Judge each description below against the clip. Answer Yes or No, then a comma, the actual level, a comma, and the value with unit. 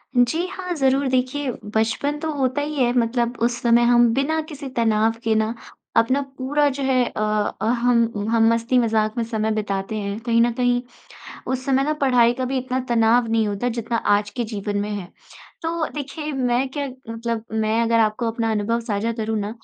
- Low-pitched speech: No, high, 235 Hz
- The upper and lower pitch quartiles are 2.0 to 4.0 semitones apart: Yes, average, 2.8 semitones